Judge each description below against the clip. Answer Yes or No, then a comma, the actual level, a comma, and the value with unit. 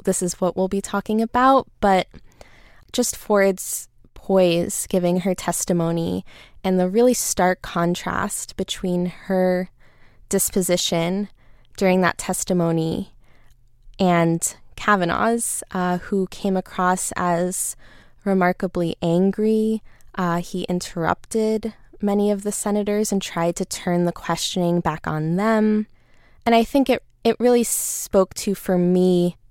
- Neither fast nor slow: No, slow, 120 wpm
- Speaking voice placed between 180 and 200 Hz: Yes, medium, 185 Hz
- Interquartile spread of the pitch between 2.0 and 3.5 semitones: Yes, average, 2.9 semitones